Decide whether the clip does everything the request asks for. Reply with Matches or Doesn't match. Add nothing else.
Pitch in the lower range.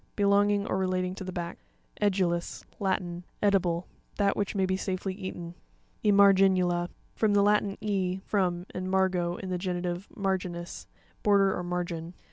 Doesn't match